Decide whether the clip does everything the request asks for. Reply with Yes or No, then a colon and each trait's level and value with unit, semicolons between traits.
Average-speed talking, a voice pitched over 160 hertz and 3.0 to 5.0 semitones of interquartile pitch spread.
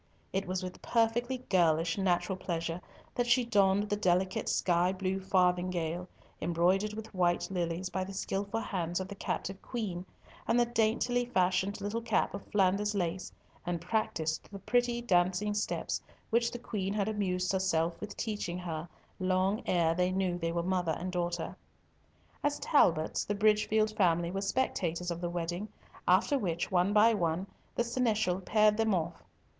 Yes: average, 160 wpm; high, 190 Hz; average, 3.3 semitones